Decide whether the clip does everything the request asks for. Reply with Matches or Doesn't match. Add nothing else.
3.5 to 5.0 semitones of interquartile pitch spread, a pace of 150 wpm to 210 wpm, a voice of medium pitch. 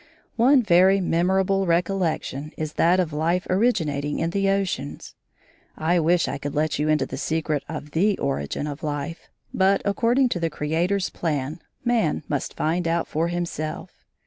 Matches